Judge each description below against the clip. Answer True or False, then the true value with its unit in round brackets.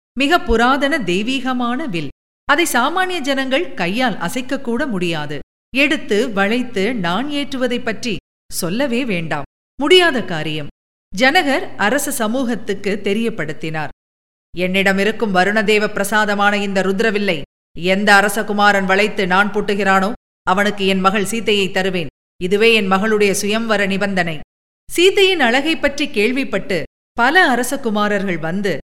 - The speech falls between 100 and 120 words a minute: True (105 wpm)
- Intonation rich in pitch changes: False (5.0 semitones)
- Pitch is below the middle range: False (210 Hz)